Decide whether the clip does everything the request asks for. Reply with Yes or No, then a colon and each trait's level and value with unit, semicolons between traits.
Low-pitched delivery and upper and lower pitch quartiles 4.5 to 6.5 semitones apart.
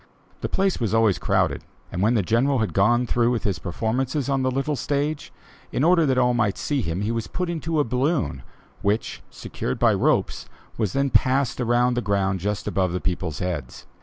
Yes: low, 120 Hz; wide, 5.5 semitones